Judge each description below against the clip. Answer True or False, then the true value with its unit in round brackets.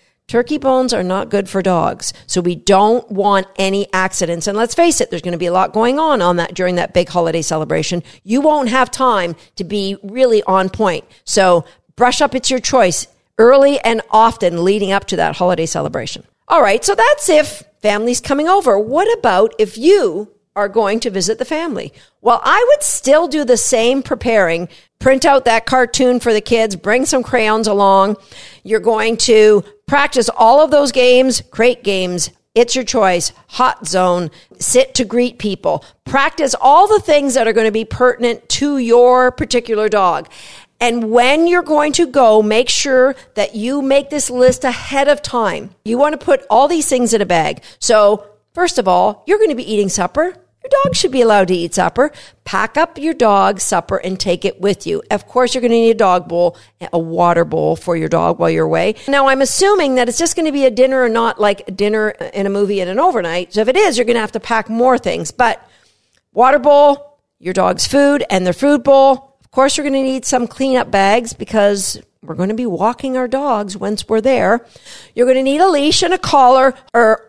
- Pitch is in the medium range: False (235 Hz)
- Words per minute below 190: False (205 wpm)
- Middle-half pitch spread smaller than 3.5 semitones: False (5.4 semitones)